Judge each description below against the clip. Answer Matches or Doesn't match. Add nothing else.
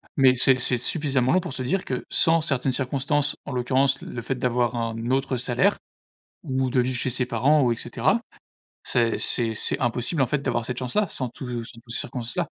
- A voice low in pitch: Matches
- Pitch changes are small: Matches